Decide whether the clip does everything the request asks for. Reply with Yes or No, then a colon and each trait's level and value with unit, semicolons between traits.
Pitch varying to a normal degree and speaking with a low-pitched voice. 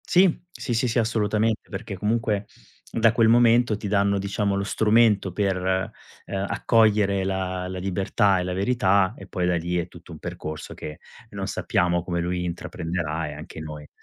Yes: average, 3.5 semitones; low, 100 Hz